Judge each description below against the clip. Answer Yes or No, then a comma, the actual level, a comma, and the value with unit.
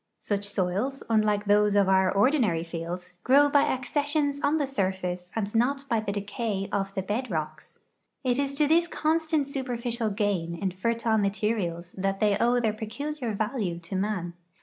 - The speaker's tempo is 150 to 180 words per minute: Yes, average, 170 wpm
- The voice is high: Yes, high, 210 Hz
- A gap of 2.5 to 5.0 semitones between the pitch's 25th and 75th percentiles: No, wide, 5.4 semitones